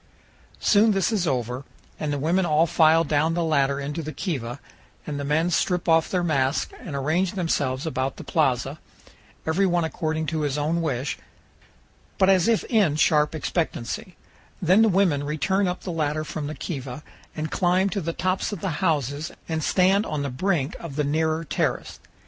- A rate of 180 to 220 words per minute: Yes, average, 185 wpm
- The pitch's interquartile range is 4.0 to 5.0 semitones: No, average, 3.6 semitones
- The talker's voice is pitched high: No, medium, 160 Hz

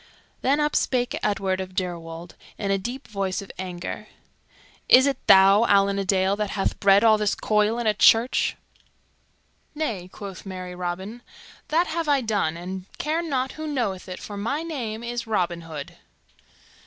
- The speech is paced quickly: No, average, 170 wpm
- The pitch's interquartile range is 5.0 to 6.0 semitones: No, average, 4.5 semitones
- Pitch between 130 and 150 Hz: No, high, 205 Hz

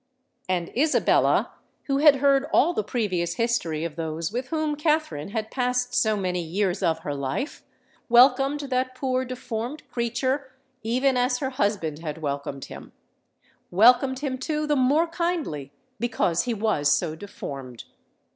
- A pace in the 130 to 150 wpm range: Yes, average, 145 wpm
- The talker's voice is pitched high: Yes, high, 240 Hz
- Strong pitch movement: Yes, wide, 7.9 semitones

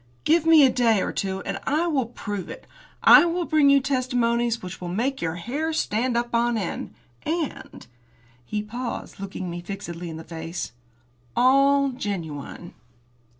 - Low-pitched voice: No, high, 235 Hz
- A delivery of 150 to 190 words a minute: Yes, average, 165 wpm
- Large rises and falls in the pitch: Yes, wide, 7.2 semitones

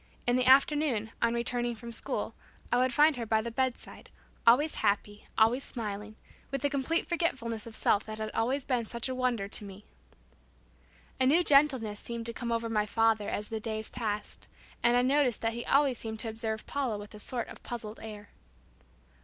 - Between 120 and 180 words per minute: No, average, 195 wpm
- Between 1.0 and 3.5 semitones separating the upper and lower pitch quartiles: Yes, average, 2.9 semitones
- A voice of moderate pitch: No, high, 235 Hz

